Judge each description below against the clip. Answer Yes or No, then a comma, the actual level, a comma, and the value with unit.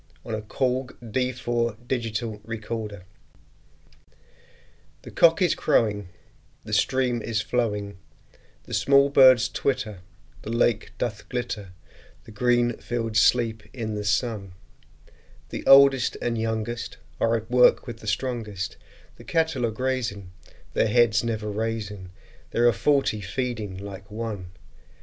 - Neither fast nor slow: No, slow, 125 wpm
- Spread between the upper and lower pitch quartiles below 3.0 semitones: Yes, narrow, 2.6 semitones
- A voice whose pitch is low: Yes, low, 115 Hz